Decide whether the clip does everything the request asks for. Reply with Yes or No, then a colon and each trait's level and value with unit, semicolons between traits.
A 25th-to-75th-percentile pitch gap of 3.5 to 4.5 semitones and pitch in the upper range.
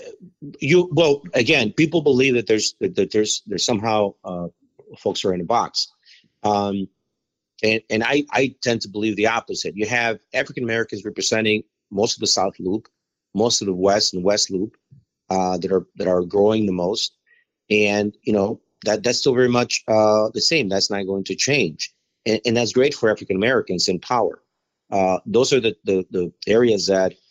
No: average, 3.8 semitones; low, 110 Hz